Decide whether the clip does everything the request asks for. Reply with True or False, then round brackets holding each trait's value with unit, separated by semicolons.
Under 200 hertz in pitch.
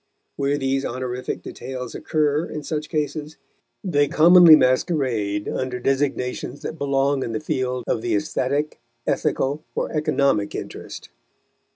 True (140 Hz)